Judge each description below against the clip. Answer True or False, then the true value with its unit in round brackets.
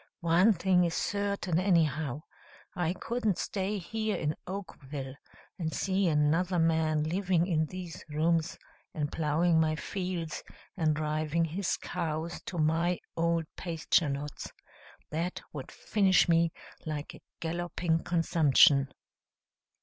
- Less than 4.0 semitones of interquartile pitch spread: True (2.6 semitones)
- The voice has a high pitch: False (165 Hz)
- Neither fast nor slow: False (120 wpm)